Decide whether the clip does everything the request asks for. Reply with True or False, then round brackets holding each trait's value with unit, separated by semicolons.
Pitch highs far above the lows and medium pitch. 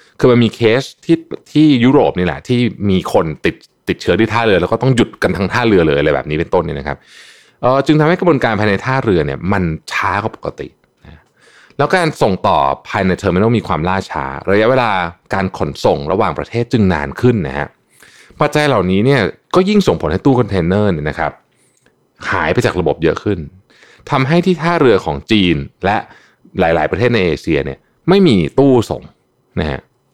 False (7.6 semitones; 115 Hz)